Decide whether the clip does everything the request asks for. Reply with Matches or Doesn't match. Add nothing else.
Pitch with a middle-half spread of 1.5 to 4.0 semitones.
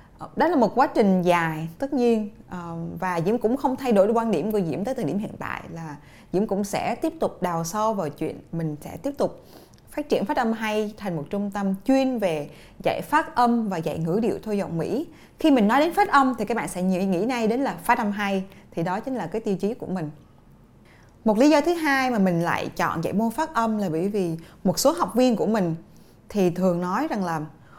Doesn't match